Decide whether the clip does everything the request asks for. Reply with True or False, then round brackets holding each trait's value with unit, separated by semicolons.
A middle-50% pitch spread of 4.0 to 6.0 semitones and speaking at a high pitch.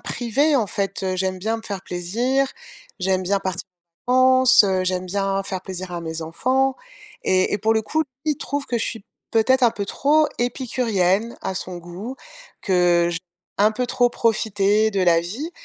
True (4.8 semitones; 205 Hz)